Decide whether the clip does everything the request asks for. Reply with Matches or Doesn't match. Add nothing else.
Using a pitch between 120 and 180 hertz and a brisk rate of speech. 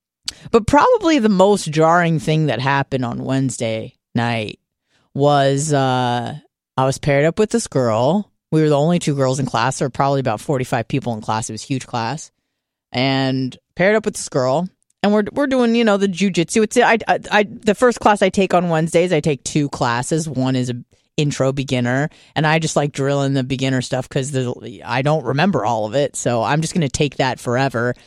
Matches